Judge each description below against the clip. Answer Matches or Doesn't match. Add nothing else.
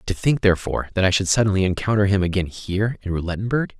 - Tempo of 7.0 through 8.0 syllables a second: Matches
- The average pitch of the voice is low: Matches